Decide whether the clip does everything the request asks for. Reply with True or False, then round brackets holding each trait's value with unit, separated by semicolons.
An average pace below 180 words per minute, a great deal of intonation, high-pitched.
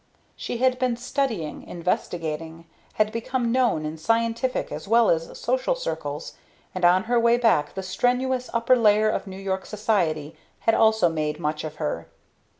True (160 wpm; 6.7 semitones; 210 Hz)